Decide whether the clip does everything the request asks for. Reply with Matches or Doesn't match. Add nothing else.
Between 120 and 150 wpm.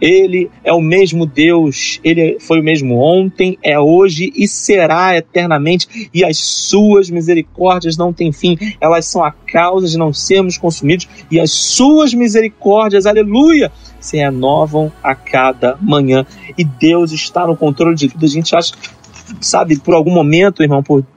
Doesn't match